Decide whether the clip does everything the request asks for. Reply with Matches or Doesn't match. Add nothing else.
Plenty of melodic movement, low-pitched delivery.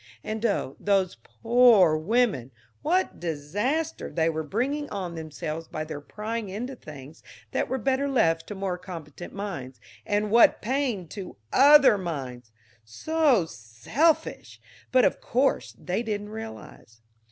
Doesn't match